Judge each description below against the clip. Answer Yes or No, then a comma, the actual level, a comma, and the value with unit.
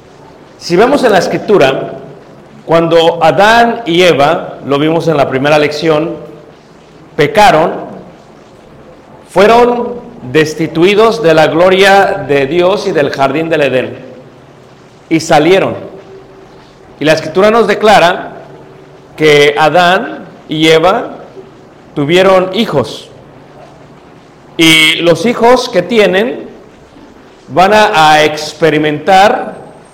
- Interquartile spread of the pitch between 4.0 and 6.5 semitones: Yes, average, 4.3 semitones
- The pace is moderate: No, slow, 100 wpm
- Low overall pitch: No, medium, 160 Hz